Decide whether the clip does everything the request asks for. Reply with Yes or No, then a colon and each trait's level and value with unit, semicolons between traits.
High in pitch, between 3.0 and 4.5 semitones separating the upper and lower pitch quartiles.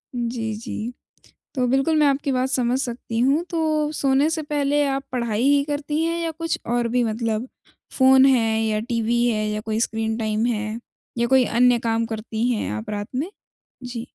Yes: high, 245 Hz; average, 3.6 semitones